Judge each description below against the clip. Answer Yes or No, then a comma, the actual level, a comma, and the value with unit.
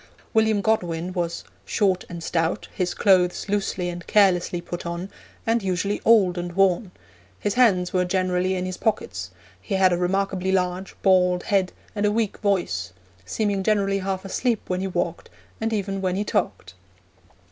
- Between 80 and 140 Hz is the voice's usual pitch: No, medium, 185 Hz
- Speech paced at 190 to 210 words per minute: No, average, 165 wpm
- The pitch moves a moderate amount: No, narrow, 2.1 semitones